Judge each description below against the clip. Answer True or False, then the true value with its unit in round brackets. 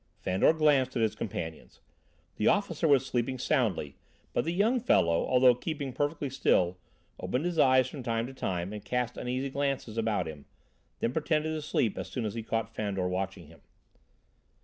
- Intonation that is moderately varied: False (5.7 semitones)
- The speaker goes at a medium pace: True (175 wpm)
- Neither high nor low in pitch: False (125 Hz)